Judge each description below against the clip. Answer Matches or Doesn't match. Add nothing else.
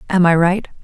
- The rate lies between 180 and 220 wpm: Matches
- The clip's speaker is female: Matches